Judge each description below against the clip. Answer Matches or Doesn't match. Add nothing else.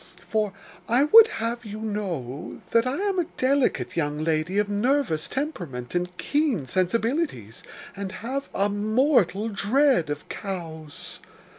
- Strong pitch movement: Matches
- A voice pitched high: Matches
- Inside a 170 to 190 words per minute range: Doesn't match